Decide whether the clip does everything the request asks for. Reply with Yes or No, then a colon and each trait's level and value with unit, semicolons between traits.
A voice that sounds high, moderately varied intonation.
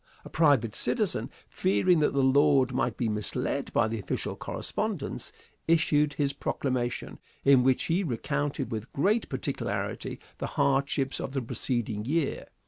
No: low, 135 Hz; average, 3.6 semitones